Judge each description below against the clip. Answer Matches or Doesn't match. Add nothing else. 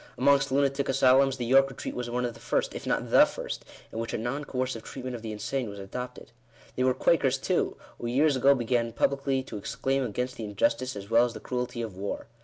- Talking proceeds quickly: Matches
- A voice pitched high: Doesn't match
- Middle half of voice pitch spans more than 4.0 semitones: Doesn't match